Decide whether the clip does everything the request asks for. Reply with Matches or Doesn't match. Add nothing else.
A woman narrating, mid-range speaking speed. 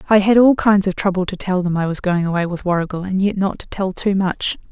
Doesn't match